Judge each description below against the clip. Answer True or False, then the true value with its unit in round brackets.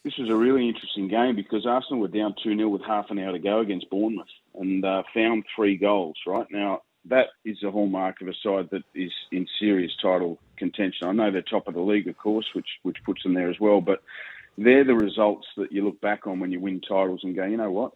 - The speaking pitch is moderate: False (100 Hz)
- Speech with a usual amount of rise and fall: False (2.2 semitones)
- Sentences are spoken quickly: True (245 wpm)